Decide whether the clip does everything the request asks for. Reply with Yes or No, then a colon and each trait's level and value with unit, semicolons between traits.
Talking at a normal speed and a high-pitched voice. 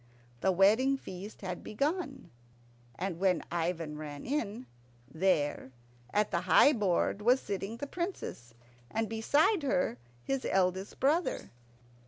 No: slow, 125 wpm; high, 200 Hz